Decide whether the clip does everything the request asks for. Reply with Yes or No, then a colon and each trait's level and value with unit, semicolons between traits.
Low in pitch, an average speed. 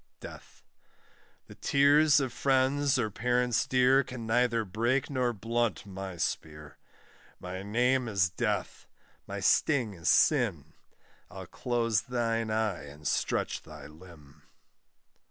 No: low, 115 Hz; slow, 120 wpm